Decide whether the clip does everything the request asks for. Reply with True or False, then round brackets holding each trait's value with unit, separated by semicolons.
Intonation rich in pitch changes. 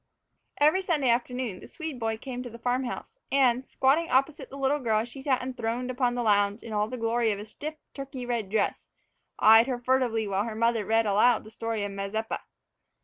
False (3.0 semitones)